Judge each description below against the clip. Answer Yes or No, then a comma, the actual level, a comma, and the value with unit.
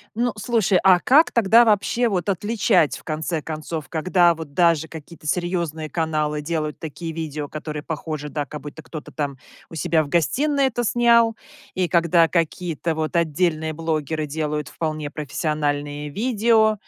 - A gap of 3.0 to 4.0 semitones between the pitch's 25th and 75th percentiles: Yes, average, 3.6 semitones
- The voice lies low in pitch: No, medium, 160 Hz